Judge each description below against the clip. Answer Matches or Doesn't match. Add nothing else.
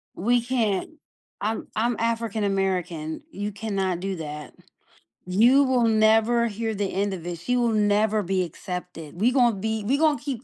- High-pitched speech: Matches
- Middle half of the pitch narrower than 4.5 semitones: Matches